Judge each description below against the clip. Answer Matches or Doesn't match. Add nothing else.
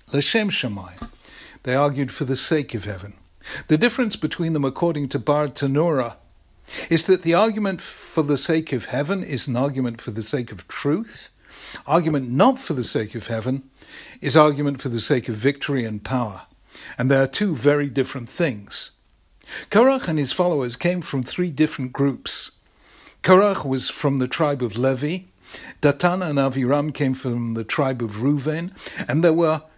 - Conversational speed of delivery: Matches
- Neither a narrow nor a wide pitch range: Matches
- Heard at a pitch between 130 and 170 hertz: Matches